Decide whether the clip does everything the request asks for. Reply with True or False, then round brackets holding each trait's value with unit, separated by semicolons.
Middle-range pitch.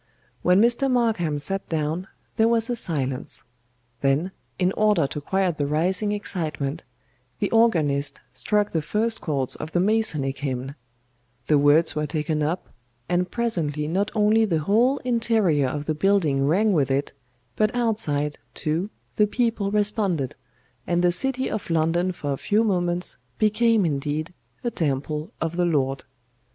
True (175 Hz)